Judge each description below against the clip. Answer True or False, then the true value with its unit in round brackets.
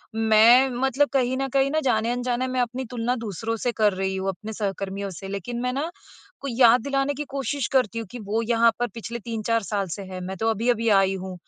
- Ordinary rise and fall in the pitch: True (3.7 semitones)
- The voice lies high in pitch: True (230 Hz)